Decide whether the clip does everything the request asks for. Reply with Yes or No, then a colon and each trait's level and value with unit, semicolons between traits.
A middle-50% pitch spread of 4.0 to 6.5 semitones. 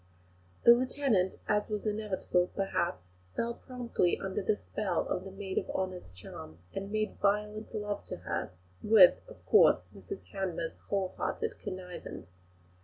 No: narrow, 2.6 semitones